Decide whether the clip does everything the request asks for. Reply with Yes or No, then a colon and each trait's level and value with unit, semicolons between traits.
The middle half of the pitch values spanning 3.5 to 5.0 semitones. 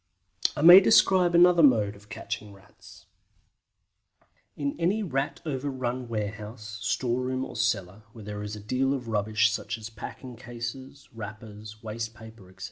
Yes: average, 3.8 semitones